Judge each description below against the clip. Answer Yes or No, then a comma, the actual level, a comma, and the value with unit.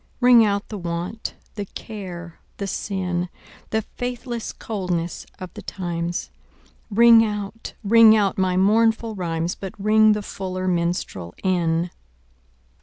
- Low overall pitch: No, high, 195 Hz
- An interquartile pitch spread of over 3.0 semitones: Yes, average, 3.8 semitones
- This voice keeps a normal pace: No, slow, 125 wpm